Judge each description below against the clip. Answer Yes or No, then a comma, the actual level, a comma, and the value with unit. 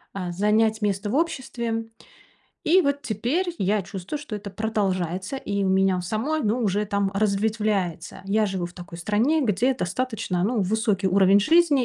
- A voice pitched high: Yes, high, 210 Hz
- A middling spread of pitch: Yes, average, 3.6 semitones